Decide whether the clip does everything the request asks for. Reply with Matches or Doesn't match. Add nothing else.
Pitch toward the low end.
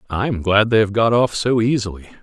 Matches